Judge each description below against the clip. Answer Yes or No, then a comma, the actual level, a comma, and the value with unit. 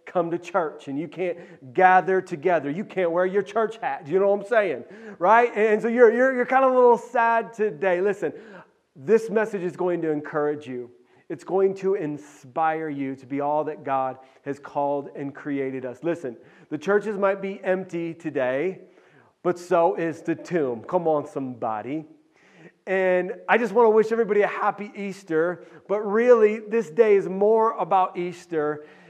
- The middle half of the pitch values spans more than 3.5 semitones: Yes, wide, 5.6 semitones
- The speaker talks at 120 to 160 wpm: No, average, 180 wpm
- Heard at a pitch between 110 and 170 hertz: No, medium, 180 Hz